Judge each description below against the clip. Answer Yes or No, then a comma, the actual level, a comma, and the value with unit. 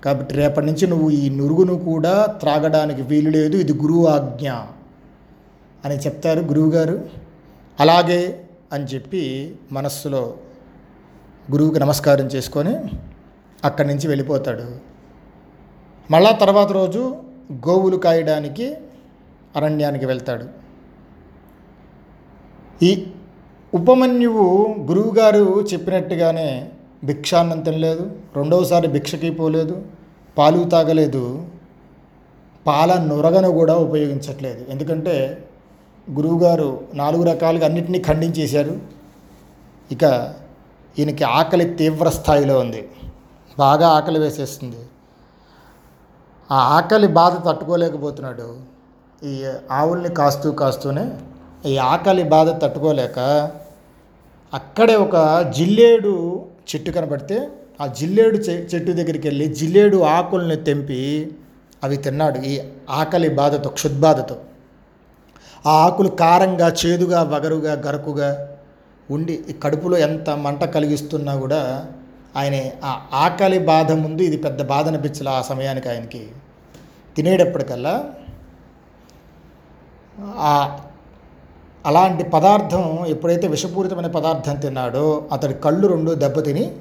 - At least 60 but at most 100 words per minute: Yes, average, 90 wpm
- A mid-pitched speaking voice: Yes, medium, 155 Hz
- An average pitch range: Yes, average, 3.5 semitones